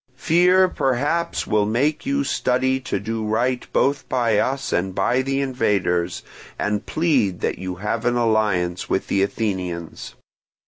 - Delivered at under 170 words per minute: Yes, average, 145 wpm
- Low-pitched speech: Yes, low, 115 Hz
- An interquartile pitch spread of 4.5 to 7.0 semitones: Yes, wide, 5.4 semitones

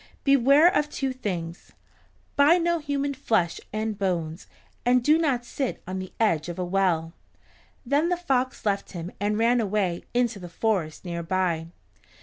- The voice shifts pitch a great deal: Yes, wide, 7.5 semitones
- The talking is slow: No, average, 160 wpm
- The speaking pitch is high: Yes, high, 215 Hz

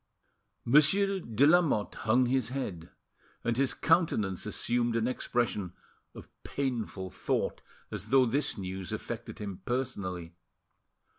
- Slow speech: Yes, slow, 120 wpm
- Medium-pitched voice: No, low, 120 Hz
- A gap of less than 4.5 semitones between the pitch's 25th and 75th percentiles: No, average, 5.3 semitones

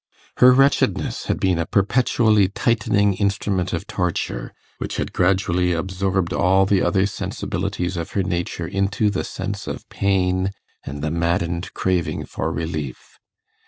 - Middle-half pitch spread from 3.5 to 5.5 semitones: No, narrow, 2.4 semitones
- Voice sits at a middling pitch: No, very low, 95 Hz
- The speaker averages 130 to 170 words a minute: Yes, average, 140 wpm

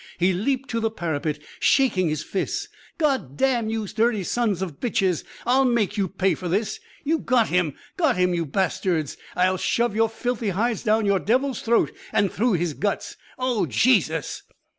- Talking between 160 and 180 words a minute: Yes, average, 175 wpm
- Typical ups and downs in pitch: Yes, average, 4.9 semitones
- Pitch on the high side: Yes, high, 210 Hz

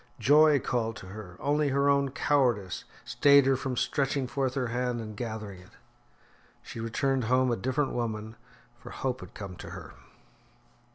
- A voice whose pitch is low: Yes, low, 125 Hz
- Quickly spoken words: No, average, 165 wpm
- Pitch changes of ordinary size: Yes, average, 3.8 semitones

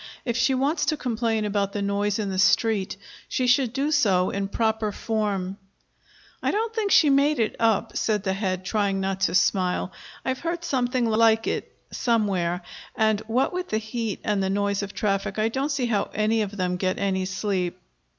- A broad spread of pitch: No, average, 3.9 semitones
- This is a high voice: Yes, high, 215 Hz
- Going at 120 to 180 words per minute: No, average, 190 wpm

